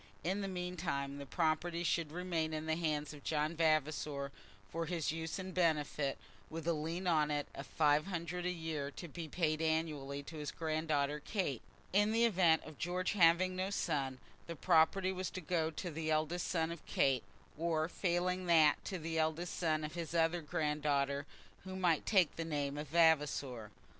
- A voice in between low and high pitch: Yes, medium, 160 Hz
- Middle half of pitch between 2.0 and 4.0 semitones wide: Yes, narrow, 2.6 semitones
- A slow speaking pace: No, average, 185 wpm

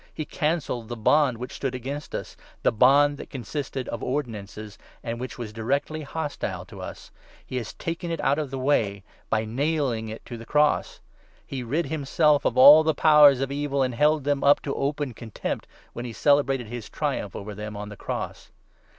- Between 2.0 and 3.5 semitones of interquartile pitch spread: No, average, 4.0 semitones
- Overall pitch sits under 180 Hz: Yes, low, 135 Hz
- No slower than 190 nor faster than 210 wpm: Yes, average, 200 wpm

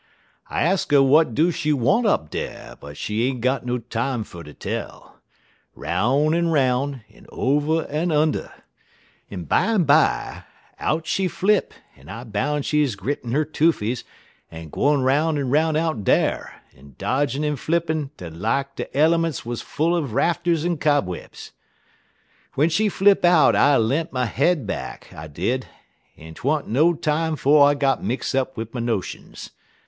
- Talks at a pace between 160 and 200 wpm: Yes, average, 165 wpm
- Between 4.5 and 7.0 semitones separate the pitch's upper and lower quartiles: Yes, average, 4.9 semitones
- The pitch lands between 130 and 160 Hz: Yes, medium, 140 Hz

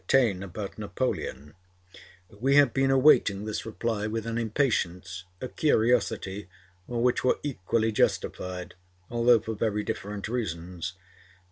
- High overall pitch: No, low, 110 Hz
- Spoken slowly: Yes, slow, 130 wpm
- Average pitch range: Yes, average, 4.2 semitones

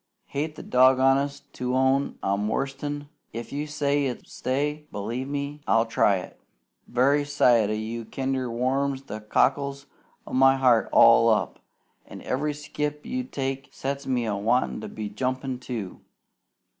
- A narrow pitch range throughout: No, average, 3.3 semitones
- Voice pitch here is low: Yes, low, 130 Hz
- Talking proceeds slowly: No, average, 155 wpm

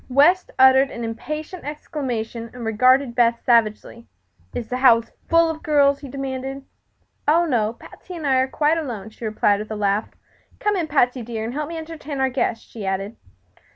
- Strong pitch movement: No, average, 4.5 semitones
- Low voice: No, very high, 260 Hz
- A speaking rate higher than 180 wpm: Yes, average, 190 wpm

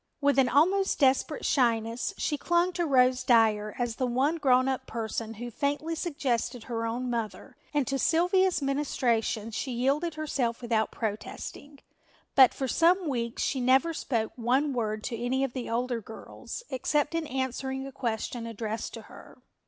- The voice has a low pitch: No, very high, 255 Hz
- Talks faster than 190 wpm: No, average, 165 wpm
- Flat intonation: No, average, 3.6 semitones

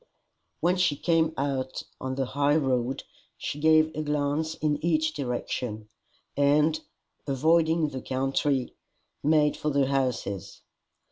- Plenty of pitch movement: No, average, 3.0 semitones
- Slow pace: Yes, slow, 125 wpm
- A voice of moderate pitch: Yes, medium, 145 Hz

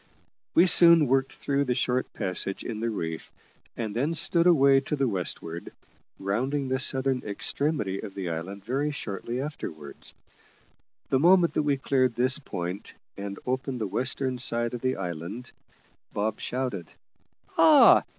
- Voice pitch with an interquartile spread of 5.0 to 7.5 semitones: Yes, wide, 5.5 semitones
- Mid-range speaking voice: No, low, 125 Hz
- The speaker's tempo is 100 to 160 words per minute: Yes, average, 150 wpm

